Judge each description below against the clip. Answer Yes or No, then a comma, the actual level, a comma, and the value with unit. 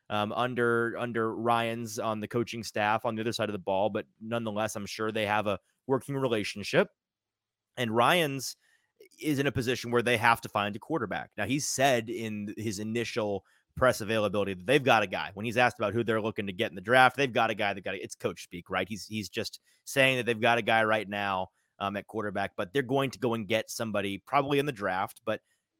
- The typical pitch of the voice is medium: No, low, 115 Hz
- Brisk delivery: Yes, fast, 235 wpm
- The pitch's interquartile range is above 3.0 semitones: No, narrow, 2.6 semitones